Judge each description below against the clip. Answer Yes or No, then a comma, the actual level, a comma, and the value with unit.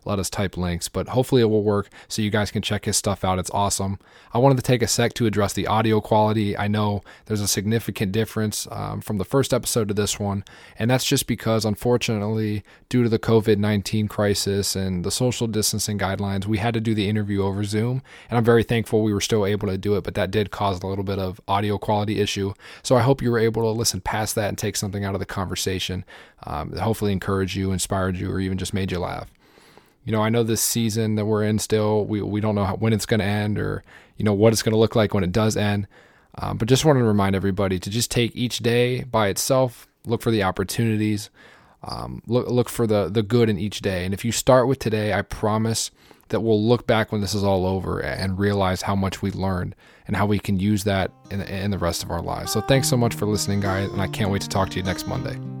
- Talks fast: Yes, fast, 255 wpm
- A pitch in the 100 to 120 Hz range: Yes, low, 105 Hz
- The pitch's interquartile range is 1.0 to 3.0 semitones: Yes, narrow, 2.4 semitones